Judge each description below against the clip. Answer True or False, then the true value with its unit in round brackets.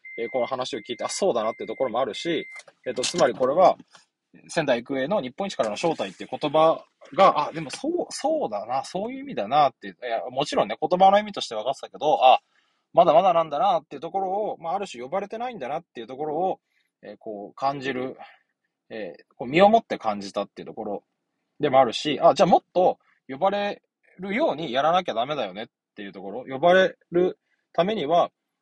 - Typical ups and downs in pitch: False (7.6 semitones)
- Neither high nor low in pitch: True (170 Hz)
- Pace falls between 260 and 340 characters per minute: False (420 characters per minute)